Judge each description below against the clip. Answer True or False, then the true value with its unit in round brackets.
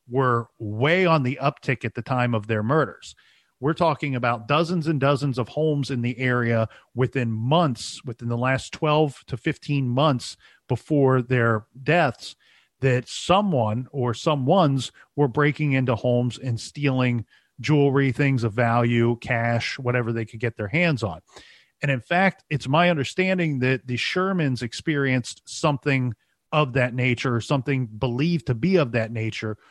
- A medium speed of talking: True (160 wpm)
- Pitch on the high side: False (130 Hz)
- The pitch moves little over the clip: False (3.7 semitones)